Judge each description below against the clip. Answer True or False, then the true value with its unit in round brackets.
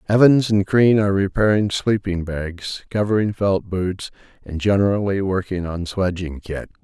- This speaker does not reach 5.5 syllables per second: True (4.6 syllables/s)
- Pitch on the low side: True (95 Hz)